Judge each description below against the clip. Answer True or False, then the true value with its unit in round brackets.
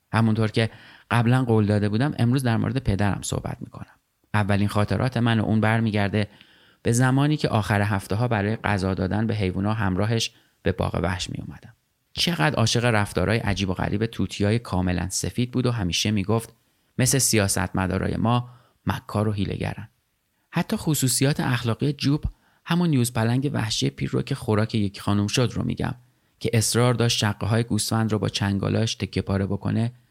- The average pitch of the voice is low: True (110 Hz)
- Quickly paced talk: True (165 wpm)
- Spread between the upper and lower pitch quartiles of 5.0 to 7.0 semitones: False (3.1 semitones)